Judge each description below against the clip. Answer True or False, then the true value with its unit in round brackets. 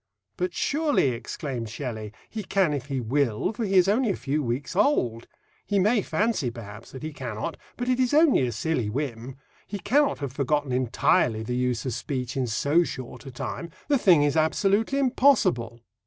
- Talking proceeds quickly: False (185 wpm)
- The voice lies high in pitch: False (145 Hz)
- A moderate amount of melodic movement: False (8.7 semitones)